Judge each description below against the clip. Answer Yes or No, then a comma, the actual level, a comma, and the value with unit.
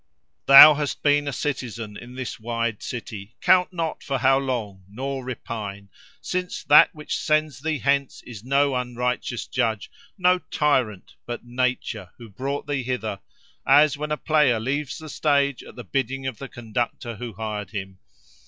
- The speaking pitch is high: No, low, 130 Hz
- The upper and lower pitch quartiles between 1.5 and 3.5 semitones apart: No, average, 4.0 semitones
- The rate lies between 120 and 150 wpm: No, average, 160 wpm